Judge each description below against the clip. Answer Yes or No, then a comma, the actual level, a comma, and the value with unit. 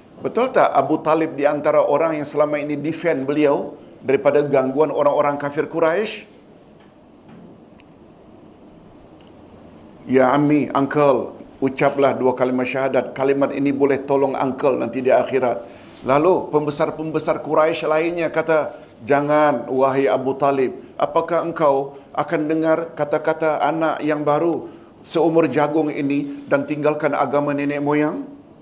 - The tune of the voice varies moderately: No, narrow, 1.9 semitones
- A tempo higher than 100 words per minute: Yes, average, 120 wpm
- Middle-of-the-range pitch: Yes, medium, 145 Hz